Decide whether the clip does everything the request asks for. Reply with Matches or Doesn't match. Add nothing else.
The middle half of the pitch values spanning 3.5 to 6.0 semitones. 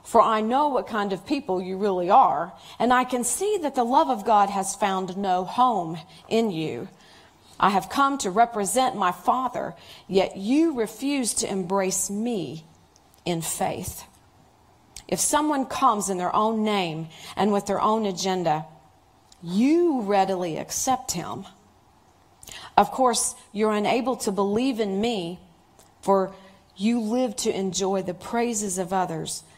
Matches